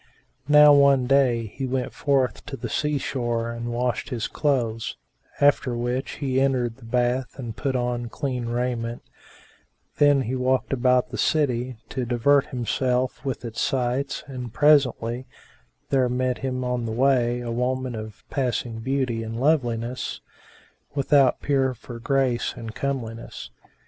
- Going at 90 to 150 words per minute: Yes, average, 145 wpm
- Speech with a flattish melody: Yes, narrow, 2.3 semitones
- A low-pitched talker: Yes, low, 125 Hz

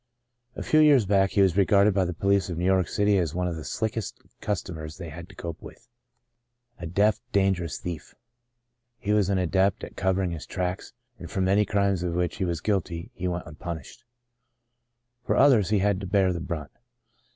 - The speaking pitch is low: Yes, very low, 95 Hz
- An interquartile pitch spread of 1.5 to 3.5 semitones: Yes, average, 2.7 semitones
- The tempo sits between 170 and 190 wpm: No, fast, 205 wpm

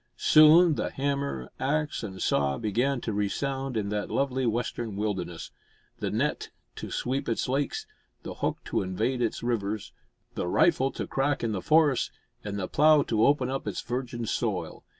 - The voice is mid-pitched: No, low, 120 Hz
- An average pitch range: Yes, average, 4.9 semitones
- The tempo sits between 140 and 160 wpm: No, average, 170 wpm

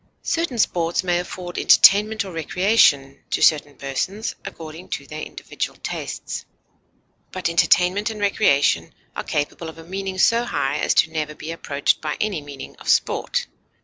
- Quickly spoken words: No, average, 155 wpm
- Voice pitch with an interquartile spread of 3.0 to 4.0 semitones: No, average, 4.7 semitones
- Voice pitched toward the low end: No, medium, 170 Hz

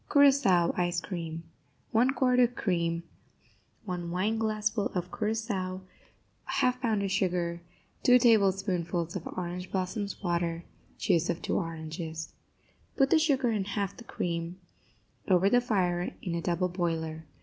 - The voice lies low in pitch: No, medium, 185 Hz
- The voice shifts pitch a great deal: No, average, 4.2 semitones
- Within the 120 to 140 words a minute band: Yes, slow, 135 wpm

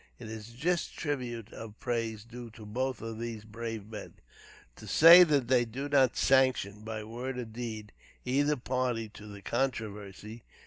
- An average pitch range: Yes, average, 3.0 semitones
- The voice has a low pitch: Yes, low, 115 Hz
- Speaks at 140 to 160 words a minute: No, average, 170 wpm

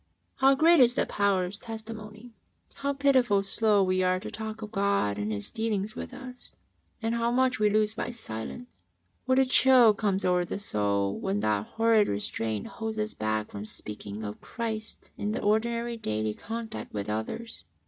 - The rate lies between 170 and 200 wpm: Yes, average, 185 wpm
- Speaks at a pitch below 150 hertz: No, high, 215 Hz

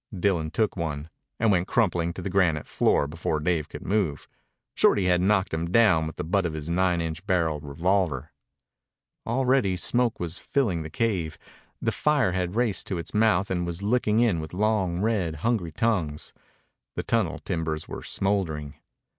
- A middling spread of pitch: Yes, average, 4.5 semitones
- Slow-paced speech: No, average, 170 wpm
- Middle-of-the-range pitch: No, very low, 90 Hz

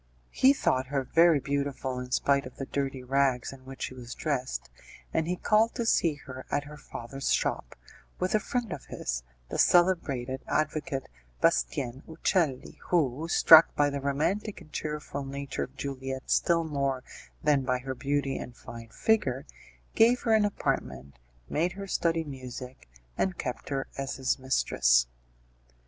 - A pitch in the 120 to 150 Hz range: Yes, medium, 140 Hz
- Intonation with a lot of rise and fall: No, average, 3.9 semitones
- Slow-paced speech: No, average, 160 wpm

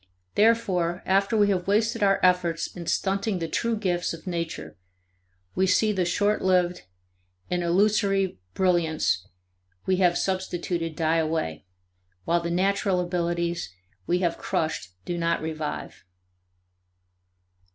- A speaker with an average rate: No, slow, 125 wpm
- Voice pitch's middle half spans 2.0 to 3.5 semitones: Yes, narrow, 2.6 semitones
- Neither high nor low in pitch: Yes, medium, 180 Hz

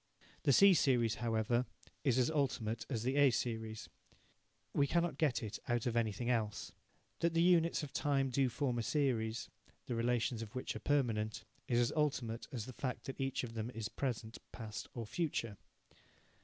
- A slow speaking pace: No, average, 180 wpm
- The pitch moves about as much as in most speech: Yes, average, 3.6 semitones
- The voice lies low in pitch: Yes, low, 120 Hz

